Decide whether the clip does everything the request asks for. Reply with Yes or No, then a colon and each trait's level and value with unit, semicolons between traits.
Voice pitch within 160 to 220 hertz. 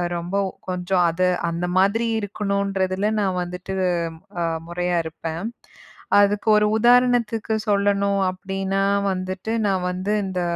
Yes: high, 195 Hz